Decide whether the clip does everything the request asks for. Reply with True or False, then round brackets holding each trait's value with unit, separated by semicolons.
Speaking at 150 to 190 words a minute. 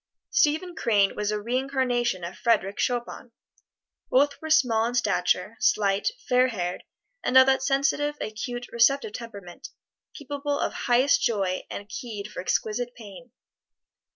False (135 wpm)